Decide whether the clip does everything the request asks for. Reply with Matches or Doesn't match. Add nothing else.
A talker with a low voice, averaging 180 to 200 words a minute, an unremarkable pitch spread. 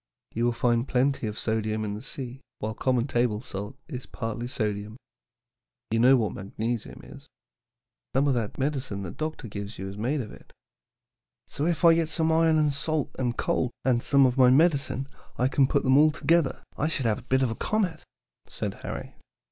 Matches